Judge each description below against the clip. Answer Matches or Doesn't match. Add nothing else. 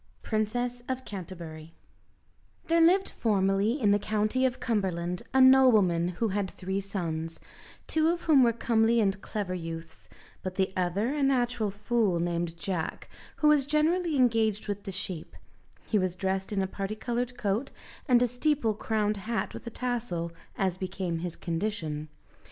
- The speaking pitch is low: Doesn't match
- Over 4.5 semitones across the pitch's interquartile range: Matches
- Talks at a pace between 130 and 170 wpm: Matches